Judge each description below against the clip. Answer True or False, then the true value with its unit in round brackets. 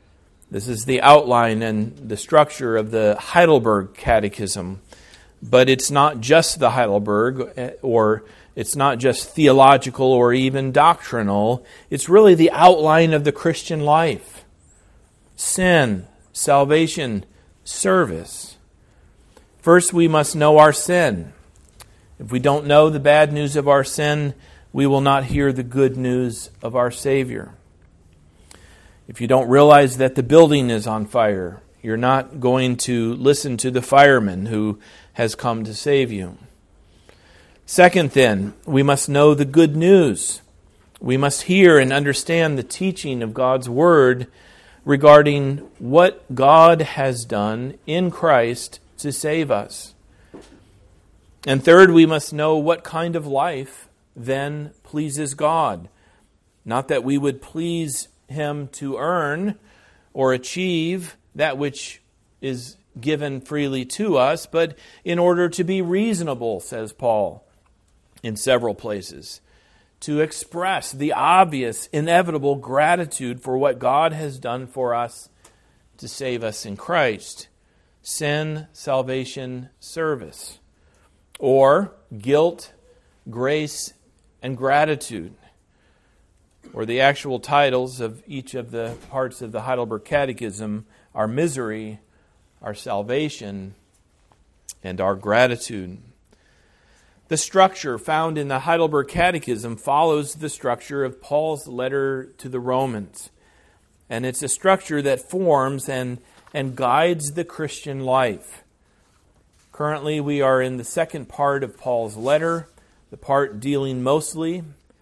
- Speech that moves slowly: True (125 wpm)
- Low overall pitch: True (130 Hz)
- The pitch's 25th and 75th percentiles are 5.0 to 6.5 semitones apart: True (5.6 semitones)